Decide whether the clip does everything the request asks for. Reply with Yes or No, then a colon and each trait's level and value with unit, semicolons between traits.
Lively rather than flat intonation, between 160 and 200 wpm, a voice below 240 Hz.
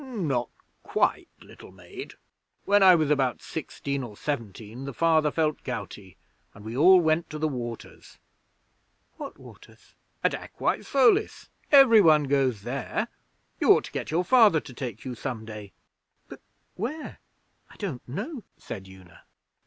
No: wide, 7.0 semitones; average, 150 wpm; medium, 140 Hz